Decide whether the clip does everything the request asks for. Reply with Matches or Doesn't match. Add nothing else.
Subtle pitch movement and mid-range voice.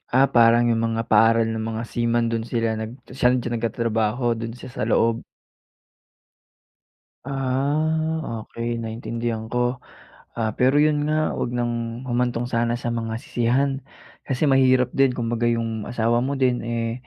Doesn't match